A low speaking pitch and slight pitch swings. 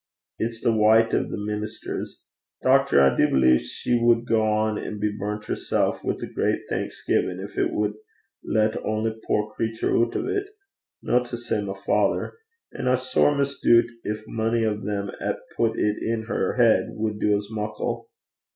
Yes: low, 110 Hz; narrow, 1.9 semitones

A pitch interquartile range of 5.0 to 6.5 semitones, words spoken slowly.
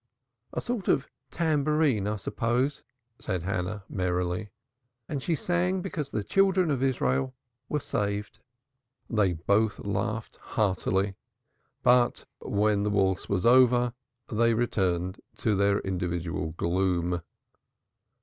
Yes: wide, 5.6 semitones; slow, 115 wpm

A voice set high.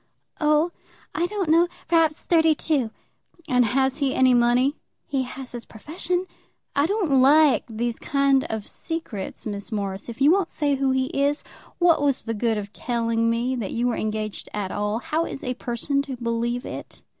Yes: very high, 260 Hz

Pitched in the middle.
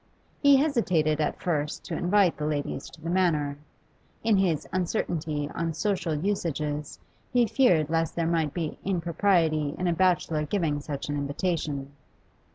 Yes: medium, 165 Hz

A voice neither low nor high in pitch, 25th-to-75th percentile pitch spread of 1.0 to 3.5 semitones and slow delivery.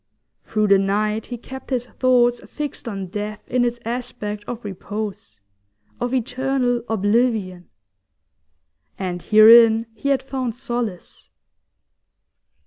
No: high, 230 Hz; average, 3.1 semitones; slow, 115 wpm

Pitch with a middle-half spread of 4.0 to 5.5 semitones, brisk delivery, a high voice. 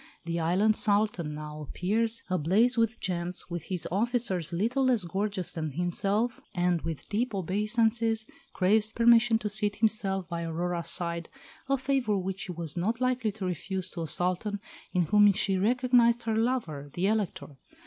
No: average, 4.5 semitones; average, 160 wpm; high, 200 Hz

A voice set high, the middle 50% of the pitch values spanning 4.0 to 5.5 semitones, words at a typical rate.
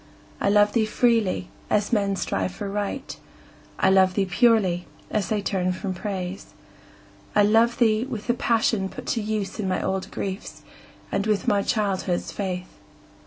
No: high, 205 Hz; narrow, 2.4 semitones; average, 165 wpm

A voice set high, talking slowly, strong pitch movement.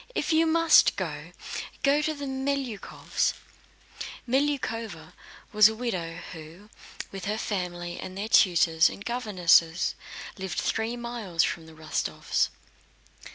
Yes: high, 210 Hz; slow, 120 wpm; wide, 6.3 semitones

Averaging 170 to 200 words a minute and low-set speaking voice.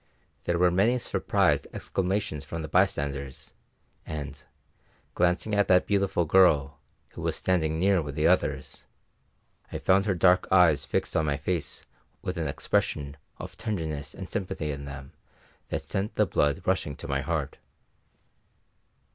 No: average, 145 wpm; very low, 80 Hz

